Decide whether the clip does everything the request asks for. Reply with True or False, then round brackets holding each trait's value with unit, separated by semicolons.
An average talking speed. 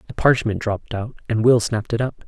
False (235 wpm)